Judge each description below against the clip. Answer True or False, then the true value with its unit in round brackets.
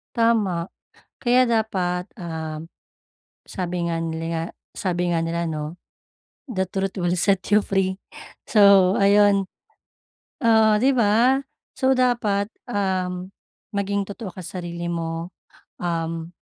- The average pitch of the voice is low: False (190 Hz)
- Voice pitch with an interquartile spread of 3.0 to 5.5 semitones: True (3.3 semitones)